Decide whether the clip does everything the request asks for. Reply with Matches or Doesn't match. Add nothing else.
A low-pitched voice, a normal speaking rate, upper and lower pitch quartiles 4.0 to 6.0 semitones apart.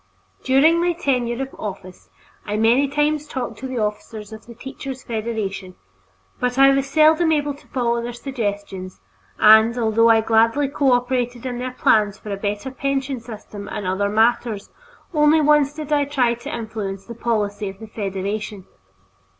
Doesn't match